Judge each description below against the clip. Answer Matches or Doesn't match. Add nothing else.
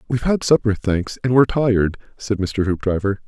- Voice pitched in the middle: Doesn't match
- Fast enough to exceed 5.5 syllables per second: Matches